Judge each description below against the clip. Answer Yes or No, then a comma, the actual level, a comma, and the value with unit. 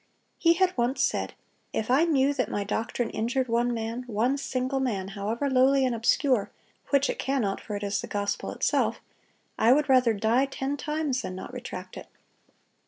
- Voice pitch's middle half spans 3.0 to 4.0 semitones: Yes, average, 3.6 semitones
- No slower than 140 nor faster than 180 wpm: Yes, average, 170 wpm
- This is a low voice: No, very high, 250 Hz